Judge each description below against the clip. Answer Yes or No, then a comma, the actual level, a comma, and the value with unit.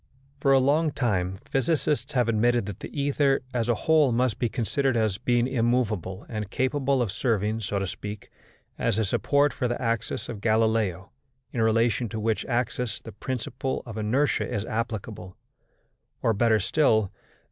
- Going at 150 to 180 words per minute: Yes, average, 170 wpm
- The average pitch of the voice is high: No, low, 115 Hz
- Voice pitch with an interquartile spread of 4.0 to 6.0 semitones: No, average, 3.1 semitones